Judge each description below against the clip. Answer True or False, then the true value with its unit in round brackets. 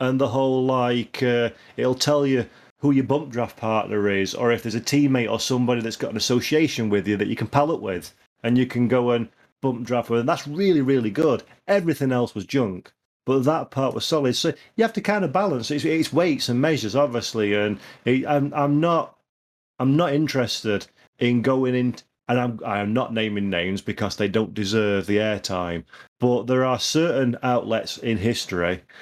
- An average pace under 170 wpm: False (205 wpm)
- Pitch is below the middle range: True (125 Hz)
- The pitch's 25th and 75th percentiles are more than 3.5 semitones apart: True (4.0 semitones)